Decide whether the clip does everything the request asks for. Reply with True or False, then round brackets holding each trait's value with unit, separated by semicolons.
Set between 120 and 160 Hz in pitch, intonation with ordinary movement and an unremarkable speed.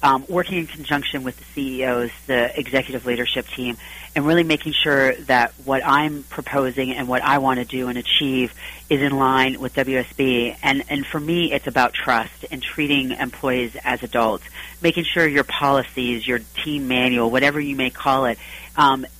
False (135 Hz; 2.3 semitones; 180 wpm)